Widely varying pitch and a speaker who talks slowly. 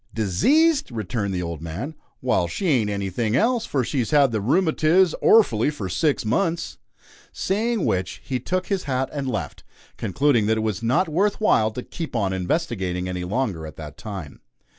No: wide, 8.7 semitones; average, 175 wpm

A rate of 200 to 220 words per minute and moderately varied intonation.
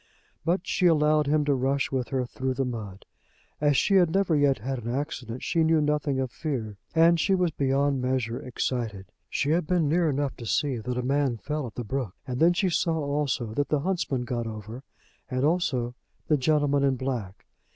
Yes: fast, 205 wpm; average, 3.7 semitones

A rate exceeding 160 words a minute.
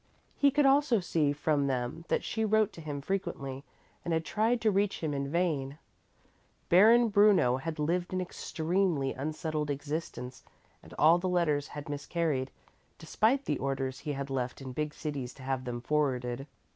Yes: average, 170 wpm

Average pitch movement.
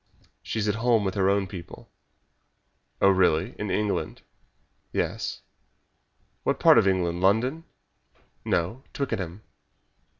Yes: average, 3.2 semitones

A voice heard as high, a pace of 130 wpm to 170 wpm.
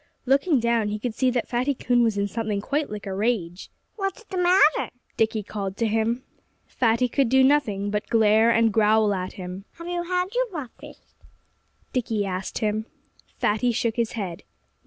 No: high, 230 Hz; average, 180 wpm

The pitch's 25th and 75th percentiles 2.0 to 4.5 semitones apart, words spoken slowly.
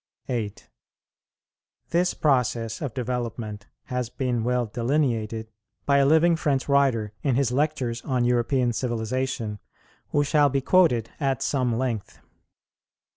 Yes: average, 3.2 semitones; slow, 130 wpm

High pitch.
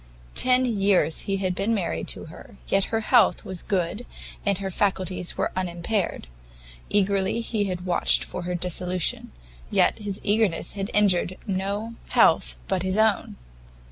Yes: high, 195 Hz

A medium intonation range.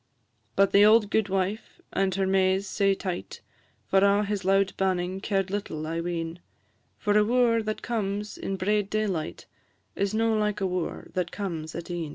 No: narrow, 2.2 semitones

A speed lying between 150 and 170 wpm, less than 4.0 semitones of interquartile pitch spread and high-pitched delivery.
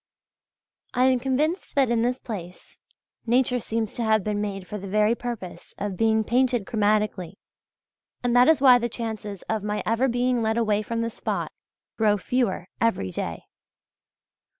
Yes: average, 165 wpm; average, 2.9 semitones; high, 225 Hz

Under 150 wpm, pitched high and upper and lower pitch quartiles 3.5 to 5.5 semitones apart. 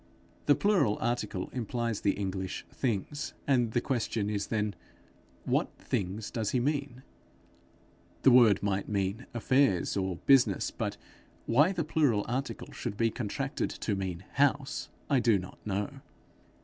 No: average, 140 wpm; low, 115 Hz; average, 4.8 semitones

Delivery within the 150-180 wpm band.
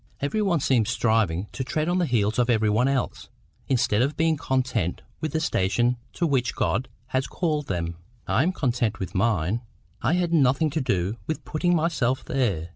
No: average, 190 wpm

